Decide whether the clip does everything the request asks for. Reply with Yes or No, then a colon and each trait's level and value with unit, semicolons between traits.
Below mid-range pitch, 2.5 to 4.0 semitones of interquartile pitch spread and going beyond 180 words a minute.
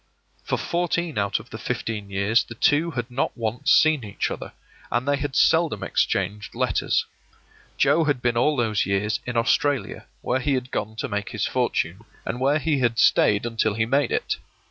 No: low, 120 Hz; average, 5.0 semitones; average, 190 wpm